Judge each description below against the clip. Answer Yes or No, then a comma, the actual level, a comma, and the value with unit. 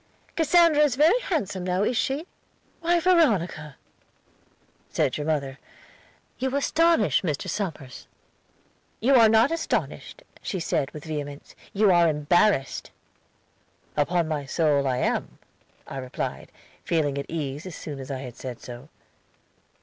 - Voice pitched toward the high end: No, medium, 170 Hz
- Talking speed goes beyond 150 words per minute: No, slow, 135 wpm